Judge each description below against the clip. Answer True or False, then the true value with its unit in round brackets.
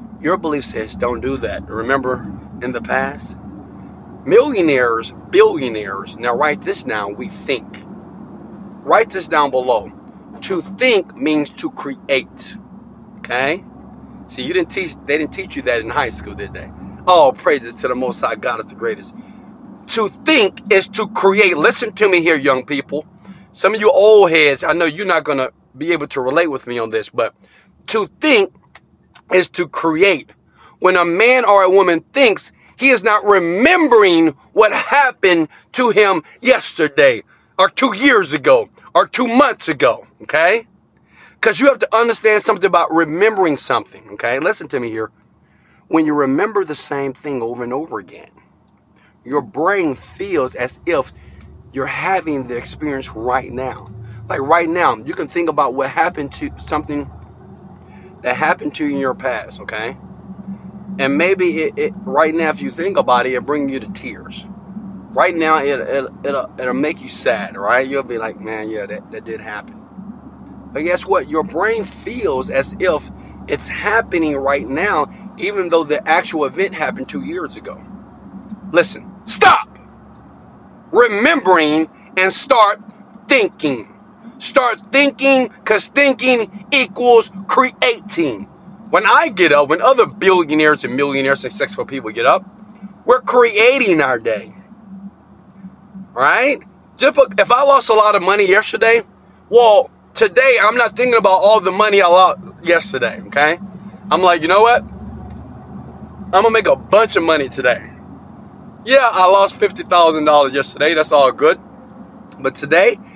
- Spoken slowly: False (160 wpm)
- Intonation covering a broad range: True (7.0 semitones)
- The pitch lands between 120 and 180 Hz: False (195 Hz)